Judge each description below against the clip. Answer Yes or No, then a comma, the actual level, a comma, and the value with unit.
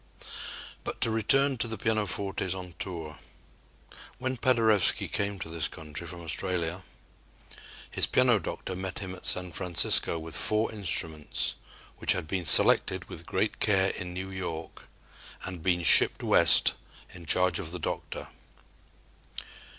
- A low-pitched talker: Yes, very low, 90 Hz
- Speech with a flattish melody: No, average, 3.3 semitones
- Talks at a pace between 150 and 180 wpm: No, average, 140 wpm